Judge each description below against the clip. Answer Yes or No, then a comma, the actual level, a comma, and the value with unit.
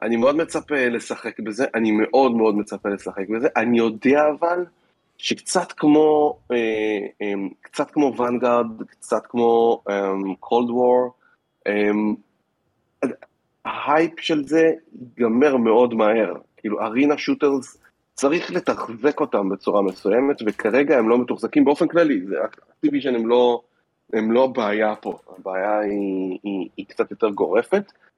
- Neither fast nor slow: Yes, average, 130 wpm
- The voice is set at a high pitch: No, low, 120 Hz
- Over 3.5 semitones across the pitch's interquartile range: Yes, wide, 5.5 semitones